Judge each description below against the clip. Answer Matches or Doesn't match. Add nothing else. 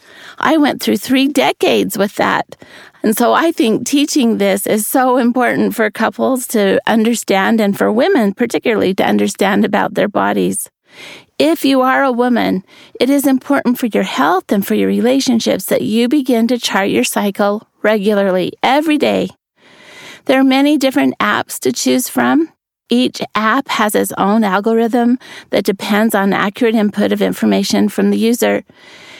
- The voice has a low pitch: Doesn't match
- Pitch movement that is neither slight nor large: Matches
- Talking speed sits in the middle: Matches